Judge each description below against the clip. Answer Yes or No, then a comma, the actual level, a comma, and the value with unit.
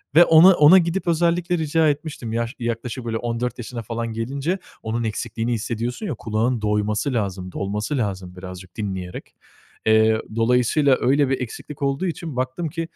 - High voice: No, low, 120 Hz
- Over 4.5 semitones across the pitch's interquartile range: Yes, average, 5.2 semitones